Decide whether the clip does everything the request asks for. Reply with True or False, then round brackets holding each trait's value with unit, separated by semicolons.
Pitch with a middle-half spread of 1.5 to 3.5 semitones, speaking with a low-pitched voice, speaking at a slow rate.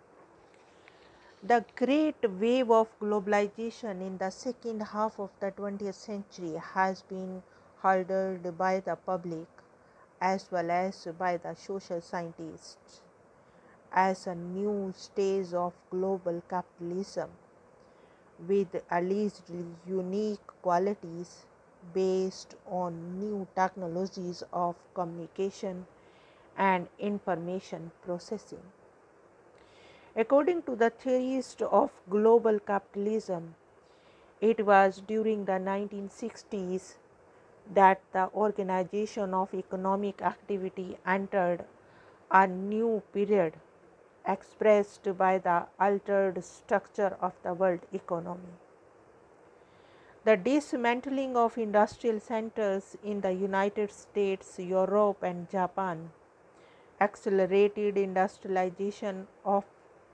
False (2.6 semitones; 195 Hz; 95 wpm)